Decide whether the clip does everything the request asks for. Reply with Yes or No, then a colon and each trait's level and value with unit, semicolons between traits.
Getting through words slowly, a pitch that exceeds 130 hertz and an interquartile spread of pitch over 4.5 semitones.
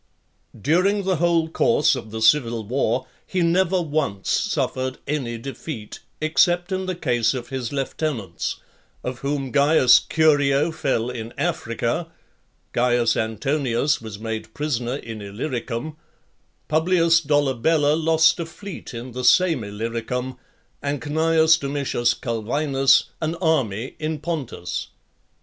Yes: slow, 125 wpm; medium, 140 Hz; average, 5.2 semitones